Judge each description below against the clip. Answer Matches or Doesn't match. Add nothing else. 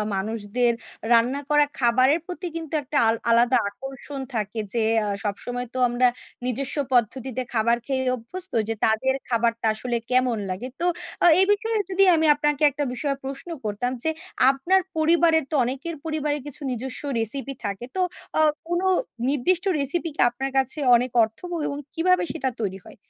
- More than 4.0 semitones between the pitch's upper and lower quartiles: Matches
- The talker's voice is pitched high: Matches